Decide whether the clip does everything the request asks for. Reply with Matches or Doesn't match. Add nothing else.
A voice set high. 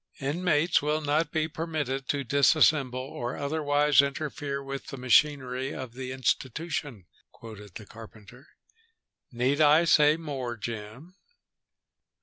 Doesn't match